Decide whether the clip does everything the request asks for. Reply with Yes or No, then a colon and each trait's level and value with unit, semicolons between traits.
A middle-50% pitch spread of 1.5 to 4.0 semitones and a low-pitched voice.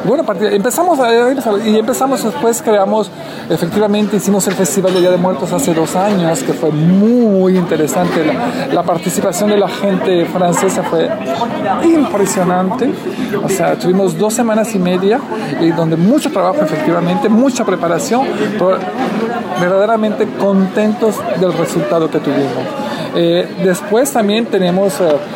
No: average, 3.3 semitones; high, 200 Hz